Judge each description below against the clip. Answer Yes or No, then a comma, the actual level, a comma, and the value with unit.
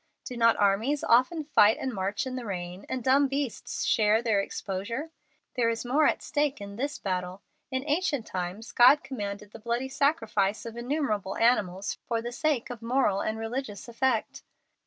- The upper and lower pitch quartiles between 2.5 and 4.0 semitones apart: No, average, 4.6 semitones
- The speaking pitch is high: Yes, high, 230 Hz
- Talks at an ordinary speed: Yes, average, 175 wpm